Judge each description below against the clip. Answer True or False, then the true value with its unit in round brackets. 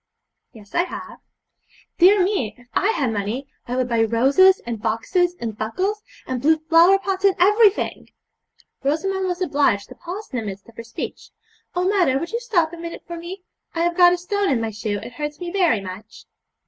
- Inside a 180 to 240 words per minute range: True (200 wpm)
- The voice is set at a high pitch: True (335 Hz)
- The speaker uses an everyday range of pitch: False (8.2 semitones)